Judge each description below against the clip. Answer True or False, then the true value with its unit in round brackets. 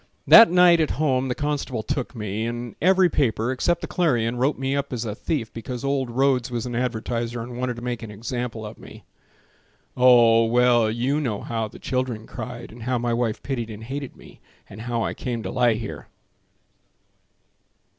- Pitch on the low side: True (120 Hz)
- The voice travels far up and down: False (2.6 semitones)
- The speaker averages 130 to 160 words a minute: False (190 wpm)